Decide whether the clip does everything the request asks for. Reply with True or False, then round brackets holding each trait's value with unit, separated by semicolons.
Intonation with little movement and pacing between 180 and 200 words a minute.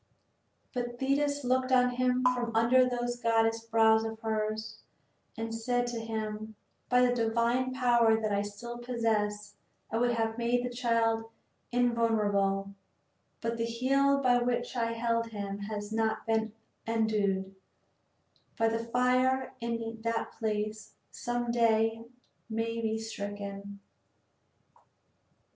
False (1.8 semitones; 135 wpm)